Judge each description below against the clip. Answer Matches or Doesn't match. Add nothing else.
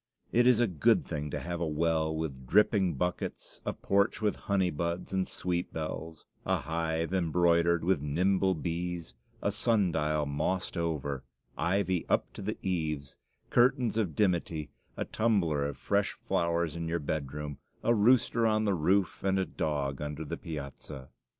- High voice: Doesn't match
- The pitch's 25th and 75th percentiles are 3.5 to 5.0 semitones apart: Matches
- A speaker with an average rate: Matches